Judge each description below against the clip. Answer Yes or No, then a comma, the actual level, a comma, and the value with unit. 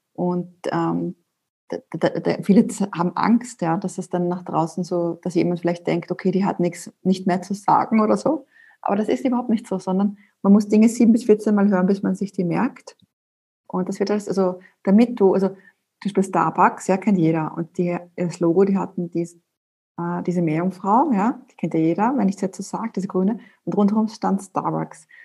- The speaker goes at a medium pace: No, fast, 215 wpm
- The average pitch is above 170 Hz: Yes, high, 190 Hz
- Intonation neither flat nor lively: Yes, average, 3.2 semitones